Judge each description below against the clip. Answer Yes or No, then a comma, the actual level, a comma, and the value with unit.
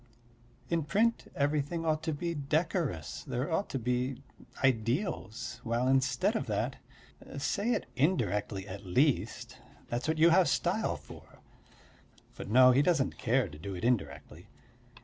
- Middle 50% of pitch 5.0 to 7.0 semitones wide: Yes, wide, 5.4 semitones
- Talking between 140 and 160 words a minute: Yes, average, 145 wpm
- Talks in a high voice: No, low, 130 Hz